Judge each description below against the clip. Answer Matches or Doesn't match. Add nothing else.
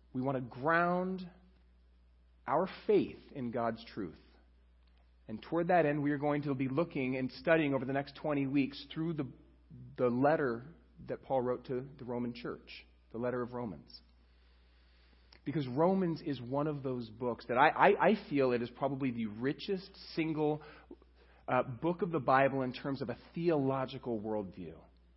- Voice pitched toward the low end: Matches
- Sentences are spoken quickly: Doesn't match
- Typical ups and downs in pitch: Doesn't match